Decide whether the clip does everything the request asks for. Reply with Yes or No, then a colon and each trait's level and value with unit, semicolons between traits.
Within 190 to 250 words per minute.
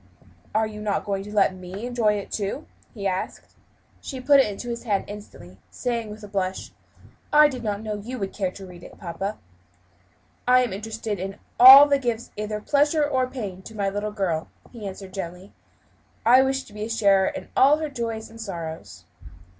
Yes: average, 195 wpm